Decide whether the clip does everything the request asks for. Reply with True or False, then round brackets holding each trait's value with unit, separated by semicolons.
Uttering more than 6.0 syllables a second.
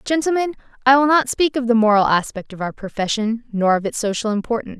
True (6.3 syllables/s)